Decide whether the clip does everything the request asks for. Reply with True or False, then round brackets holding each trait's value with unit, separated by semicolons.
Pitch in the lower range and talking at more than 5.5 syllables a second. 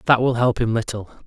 True (120 Hz; 5.9 syllables/s)